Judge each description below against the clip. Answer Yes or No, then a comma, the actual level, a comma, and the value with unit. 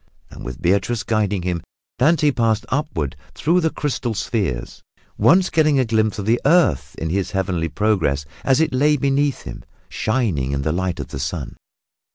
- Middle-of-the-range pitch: No, low, 110 Hz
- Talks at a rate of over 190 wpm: No, average, 175 wpm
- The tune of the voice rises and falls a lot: Yes, wide, 7.8 semitones